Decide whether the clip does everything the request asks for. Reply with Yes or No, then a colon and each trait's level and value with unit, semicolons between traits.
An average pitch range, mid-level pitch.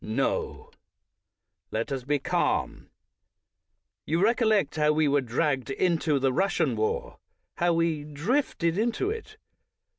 No: wide, 7.3 semitones; medium, 165 Hz